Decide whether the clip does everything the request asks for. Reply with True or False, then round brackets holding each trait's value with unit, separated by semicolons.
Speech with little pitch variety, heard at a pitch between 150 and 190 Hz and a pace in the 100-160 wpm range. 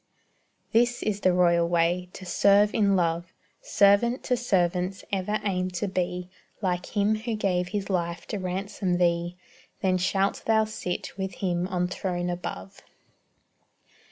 True (2.3 semitones; 185 Hz; 145 wpm)